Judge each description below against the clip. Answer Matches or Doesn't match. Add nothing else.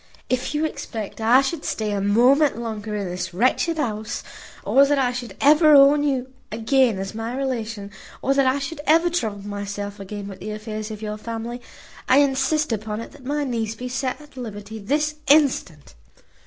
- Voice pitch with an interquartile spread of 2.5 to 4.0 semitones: Doesn't match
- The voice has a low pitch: Doesn't match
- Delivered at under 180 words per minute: Doesn't match